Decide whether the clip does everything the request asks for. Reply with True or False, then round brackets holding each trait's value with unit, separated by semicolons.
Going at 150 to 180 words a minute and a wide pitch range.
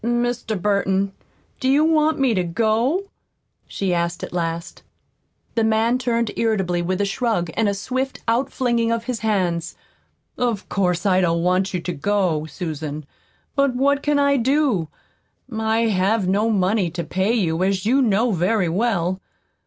False (160 wpm; 4.8 semitones)